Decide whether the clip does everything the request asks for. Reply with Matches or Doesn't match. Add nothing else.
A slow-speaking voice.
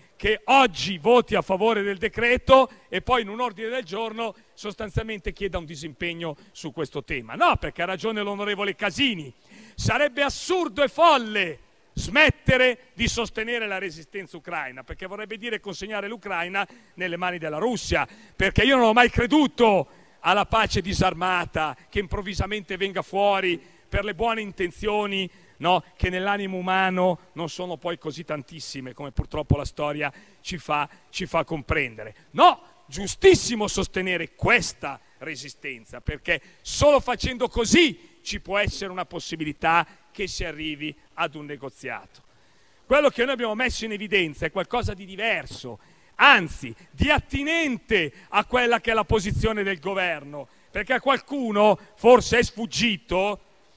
Doesn't match